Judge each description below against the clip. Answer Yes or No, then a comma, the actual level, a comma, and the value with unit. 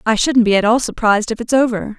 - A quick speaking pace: Yes, fast, 270 wpm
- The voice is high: Yes, high, 225 Hz